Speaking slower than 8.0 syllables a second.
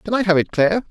No: 8.1 syllables/s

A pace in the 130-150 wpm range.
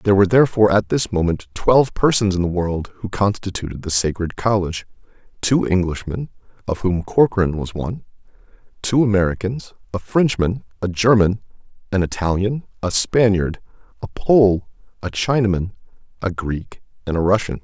Yes: average, 140 wpm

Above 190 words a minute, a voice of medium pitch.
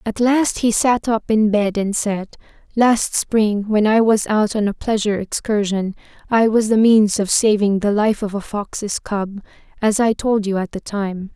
No: average, 200 wpm; high, 210 Hz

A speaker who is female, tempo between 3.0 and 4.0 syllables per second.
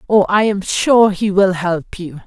Yes: female; 3.9 syllables/s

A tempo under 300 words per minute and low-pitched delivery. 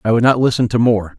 No: fast, 305 wpm; low, 115 Hz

